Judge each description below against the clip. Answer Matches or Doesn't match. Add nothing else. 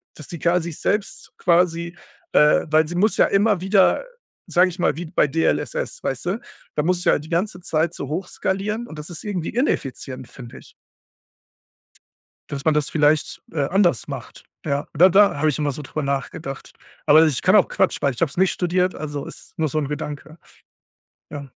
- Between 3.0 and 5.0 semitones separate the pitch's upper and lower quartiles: Matches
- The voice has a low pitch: Doesn't match